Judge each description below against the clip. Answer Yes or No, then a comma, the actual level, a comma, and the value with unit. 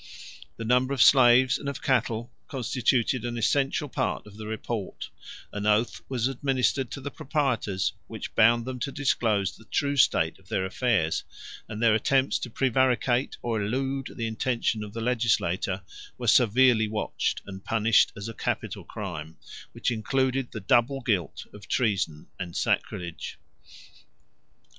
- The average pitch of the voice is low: Yes, low, 115 Hz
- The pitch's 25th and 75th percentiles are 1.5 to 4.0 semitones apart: Yes, average, 3.7 semitones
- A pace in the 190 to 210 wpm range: No, average, 150 wpm